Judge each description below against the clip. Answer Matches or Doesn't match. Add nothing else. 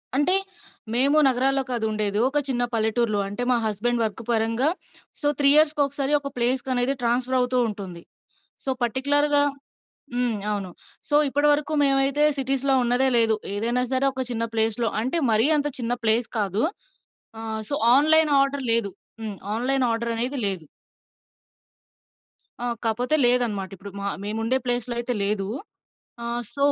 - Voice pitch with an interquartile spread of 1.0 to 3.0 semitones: Doesn't match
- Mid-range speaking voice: Doesn't match